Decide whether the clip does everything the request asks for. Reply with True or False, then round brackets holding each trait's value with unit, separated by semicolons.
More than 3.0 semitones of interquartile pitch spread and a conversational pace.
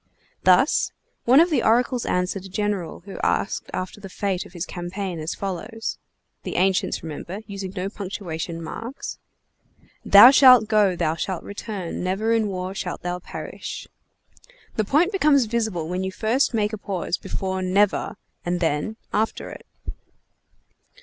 True (3.4 semitones; 150 wpm)